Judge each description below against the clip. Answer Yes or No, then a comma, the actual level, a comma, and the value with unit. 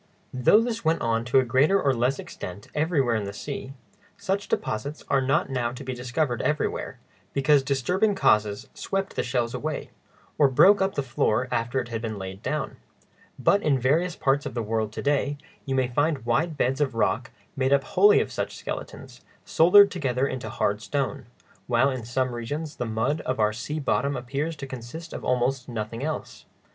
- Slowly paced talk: No, average, 190 wpm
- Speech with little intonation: No, average, 4.1 semitones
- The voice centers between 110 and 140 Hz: Yes, low, 135 Hz